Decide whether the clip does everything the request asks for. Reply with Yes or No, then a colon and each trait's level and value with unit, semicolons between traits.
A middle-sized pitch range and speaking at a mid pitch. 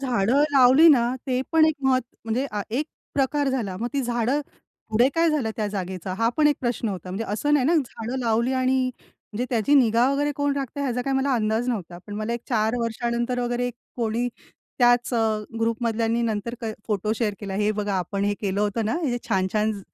No: average, 3.3 semitones; high, 235 Hz